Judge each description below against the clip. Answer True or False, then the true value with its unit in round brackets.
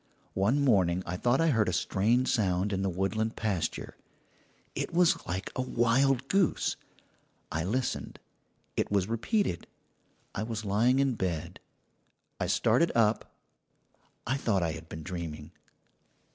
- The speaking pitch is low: True (105 Hz)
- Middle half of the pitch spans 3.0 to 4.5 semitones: False (5.5 semitones)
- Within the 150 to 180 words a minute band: False (140 wpm)